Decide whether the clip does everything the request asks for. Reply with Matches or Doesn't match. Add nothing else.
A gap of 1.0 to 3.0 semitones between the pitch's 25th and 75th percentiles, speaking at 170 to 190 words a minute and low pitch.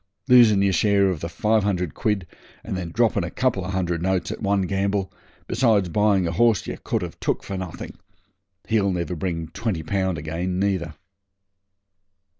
Matches